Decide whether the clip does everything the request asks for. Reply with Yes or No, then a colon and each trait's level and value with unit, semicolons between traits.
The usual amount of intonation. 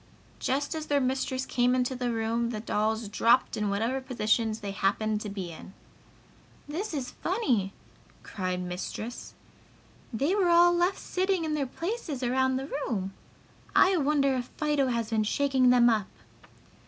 Yes: average, 4.9 semitones